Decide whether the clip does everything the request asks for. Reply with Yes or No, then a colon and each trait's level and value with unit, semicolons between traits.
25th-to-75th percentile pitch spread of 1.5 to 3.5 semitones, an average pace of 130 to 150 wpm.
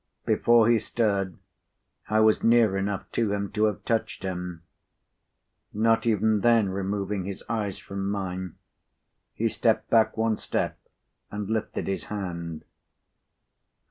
Yes: narrow, 2.4 semitones; slow, 135 wpm